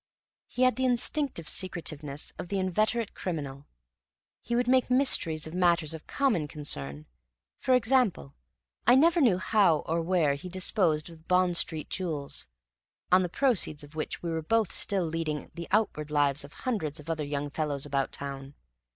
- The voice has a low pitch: No, medium, 170 Hz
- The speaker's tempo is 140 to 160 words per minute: No, average, 170 wpm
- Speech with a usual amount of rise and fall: No, wide, 6.2 semitones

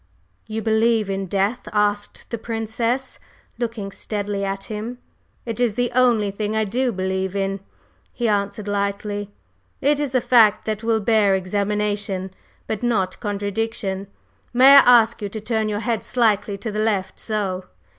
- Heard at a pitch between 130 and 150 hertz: No, high, 210 Hz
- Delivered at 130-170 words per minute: Yes, average, 155 wpm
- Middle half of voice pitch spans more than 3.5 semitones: No, narrow, 2.4 semitones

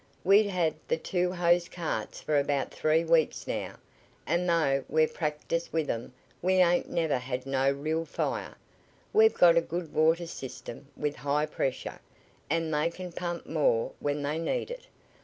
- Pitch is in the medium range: Yes, medium, 165 Hz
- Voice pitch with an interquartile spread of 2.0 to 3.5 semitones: Yes, average, 3.2 semitones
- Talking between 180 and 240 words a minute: No, average, 165 wpm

